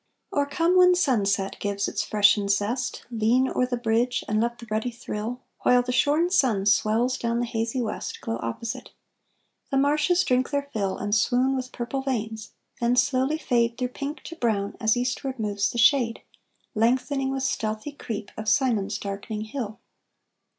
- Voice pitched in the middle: No, high, 240 Hz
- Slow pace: No, average, 170 wpm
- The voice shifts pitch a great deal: No, average, 3.7 semitones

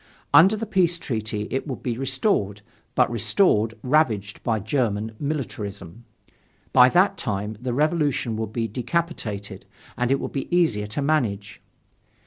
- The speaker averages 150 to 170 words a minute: No, average, 140 wpm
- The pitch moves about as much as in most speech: No, wide, 6.2 semitones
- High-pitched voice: No, low, 120 Hz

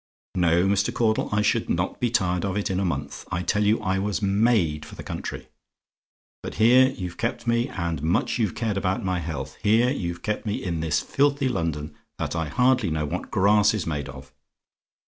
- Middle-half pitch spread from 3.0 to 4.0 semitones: No, average, 4.9 semitones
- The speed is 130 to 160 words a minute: No, average, 200 wpm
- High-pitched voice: No, very low, 95 Hz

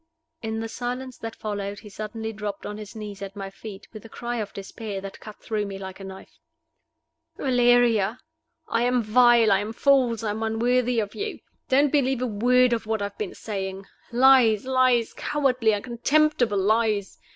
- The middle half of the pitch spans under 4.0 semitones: Yes, average, 3.1 semitones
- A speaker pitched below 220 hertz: No, high, 225 Hz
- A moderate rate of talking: Yes, average, 185 wpm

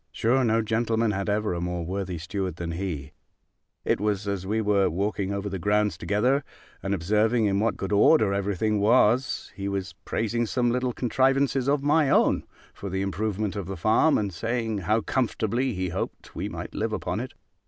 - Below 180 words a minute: No, average, 190 wpm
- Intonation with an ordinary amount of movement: Yes, average, 3.1 semitones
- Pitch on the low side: Yes, low, 105 Hz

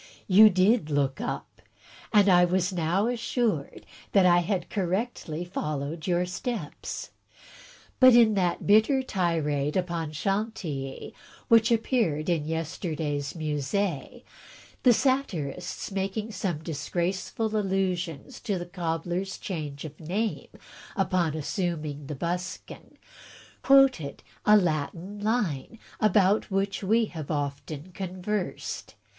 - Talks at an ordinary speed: No, slow, 115 wpm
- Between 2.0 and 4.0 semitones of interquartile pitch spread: No, average, 4.9 semitones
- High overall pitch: No, medium, 180 Hz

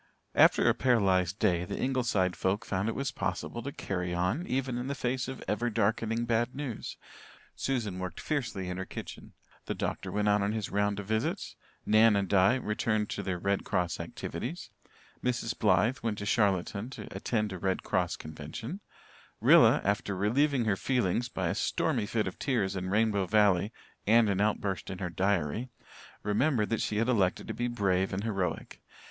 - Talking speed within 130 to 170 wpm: No, average, 180 wpm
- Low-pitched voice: Yes, low, 105 Hz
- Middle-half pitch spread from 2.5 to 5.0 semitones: Yes, average, 3.9 semitones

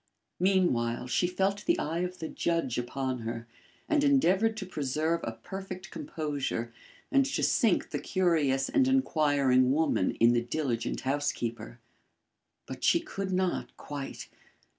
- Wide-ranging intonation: Yes, wide, 6.6 semitones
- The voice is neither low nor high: Yes, medium, 160 Hz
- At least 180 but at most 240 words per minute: No, average, 140 wpm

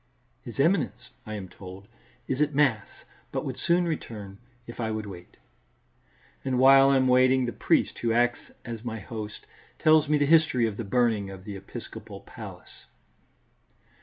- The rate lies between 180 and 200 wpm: No, average, 165 wpm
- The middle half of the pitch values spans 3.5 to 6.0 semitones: Yes, average, 4.4 semitones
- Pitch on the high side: No, low, 120 Hz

